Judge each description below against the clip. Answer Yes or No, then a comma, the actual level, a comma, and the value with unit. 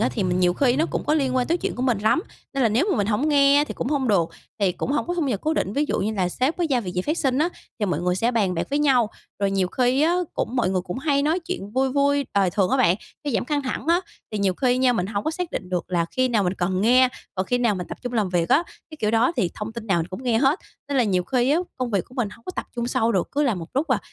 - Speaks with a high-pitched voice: Yes, high, 240 Hz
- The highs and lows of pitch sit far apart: Yes, wide, 6.3 semitones